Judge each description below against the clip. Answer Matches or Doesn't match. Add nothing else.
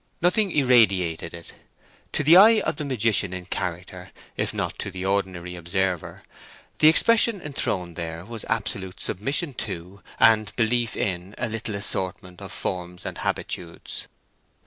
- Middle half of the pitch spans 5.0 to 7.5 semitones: Matches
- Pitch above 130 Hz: Doesn't match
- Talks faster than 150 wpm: Doesn't match